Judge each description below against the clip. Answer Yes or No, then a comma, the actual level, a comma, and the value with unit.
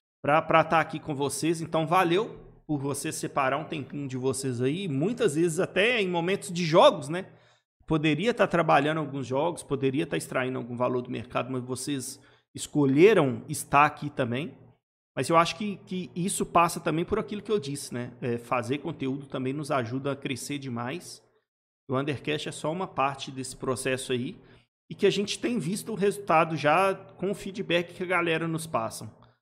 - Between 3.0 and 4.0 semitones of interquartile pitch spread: No, average, 4.6 semitones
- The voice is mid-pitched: Yes, medium, 150 Hz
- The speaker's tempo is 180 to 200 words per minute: Yes, fast, 185 wpm